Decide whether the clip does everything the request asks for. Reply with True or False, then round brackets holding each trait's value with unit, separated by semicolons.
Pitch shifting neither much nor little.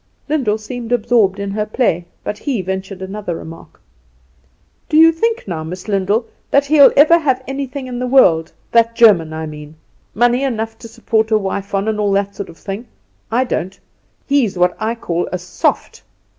True (4.8 semitones)